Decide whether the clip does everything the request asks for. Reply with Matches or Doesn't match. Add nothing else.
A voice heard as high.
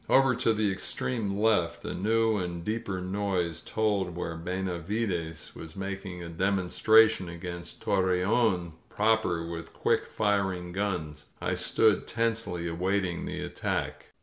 Doesn't match